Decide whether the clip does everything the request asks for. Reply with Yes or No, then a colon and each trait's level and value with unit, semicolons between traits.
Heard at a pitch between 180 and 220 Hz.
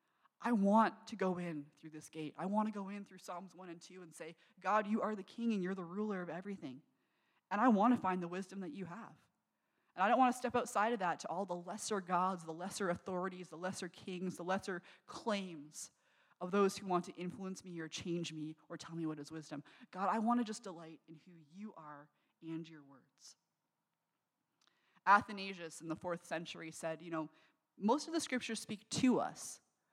Yes: medium, 185 Hz